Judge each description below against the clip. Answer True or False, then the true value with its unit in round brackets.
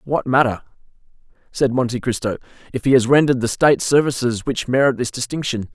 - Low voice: True (125 Hz)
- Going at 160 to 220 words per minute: True (165 wpm)